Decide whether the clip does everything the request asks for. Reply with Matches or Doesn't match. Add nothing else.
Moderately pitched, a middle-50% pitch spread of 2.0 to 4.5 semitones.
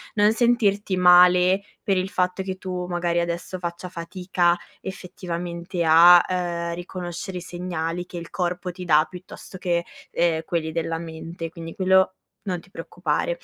Doesn't match